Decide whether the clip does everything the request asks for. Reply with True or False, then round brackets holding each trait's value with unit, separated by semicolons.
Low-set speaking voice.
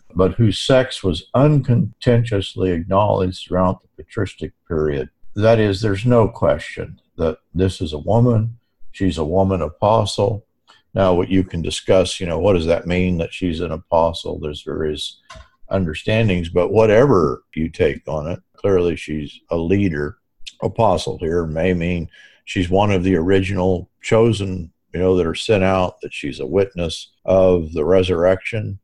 True (95 Hz)